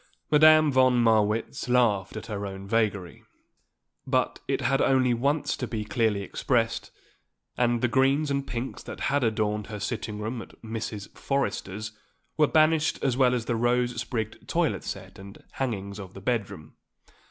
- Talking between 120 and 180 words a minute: Yes, average, 165 wpm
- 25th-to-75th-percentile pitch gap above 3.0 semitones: Yes, average, 3.6 semitones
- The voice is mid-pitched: No, low, 115 Hz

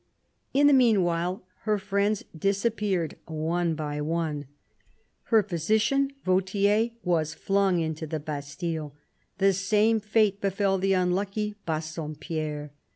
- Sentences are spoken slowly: Yes, slow, 110 wpm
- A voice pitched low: No, medium, 185 Hz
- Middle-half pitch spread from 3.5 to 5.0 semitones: Yes, average, 4.5 semitones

